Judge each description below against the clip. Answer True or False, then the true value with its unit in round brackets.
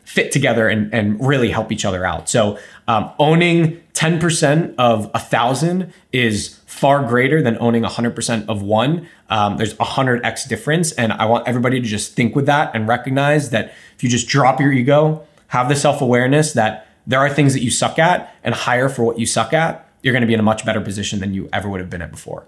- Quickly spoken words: True (220 wpm)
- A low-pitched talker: True (120 Hz)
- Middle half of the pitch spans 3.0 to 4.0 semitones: False (4.7 semitones)